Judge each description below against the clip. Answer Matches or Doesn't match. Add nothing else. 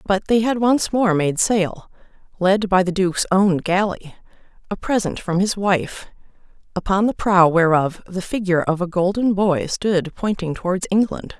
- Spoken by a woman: Matches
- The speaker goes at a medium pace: Matches